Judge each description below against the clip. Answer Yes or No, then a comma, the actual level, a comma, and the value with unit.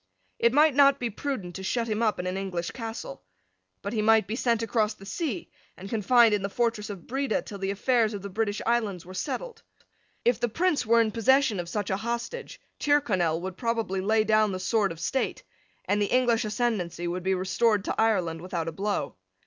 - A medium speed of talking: No, fast, 210 wpm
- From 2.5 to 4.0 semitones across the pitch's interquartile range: Yes, average, 3.7 semitones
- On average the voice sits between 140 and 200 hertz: No, high, 215 Hz